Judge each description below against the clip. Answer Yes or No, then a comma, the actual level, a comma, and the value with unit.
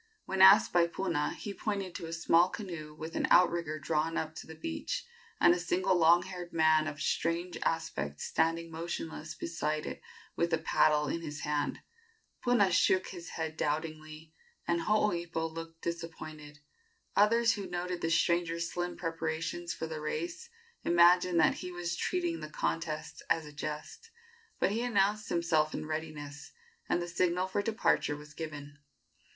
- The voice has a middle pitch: Yes, medium, 165 Hz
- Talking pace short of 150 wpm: No, average, 160 wpm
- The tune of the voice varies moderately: No, narrow, 2.3 semitones